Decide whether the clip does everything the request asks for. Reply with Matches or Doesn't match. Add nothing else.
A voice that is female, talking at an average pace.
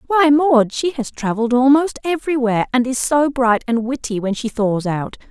Matches